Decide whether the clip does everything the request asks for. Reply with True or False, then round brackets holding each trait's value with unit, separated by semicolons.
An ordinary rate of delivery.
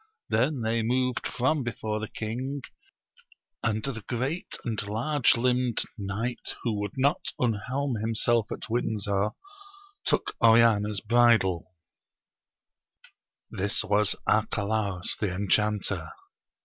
False (105 wpm)